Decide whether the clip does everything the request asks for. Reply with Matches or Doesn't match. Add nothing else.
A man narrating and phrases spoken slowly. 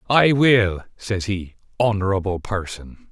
Matches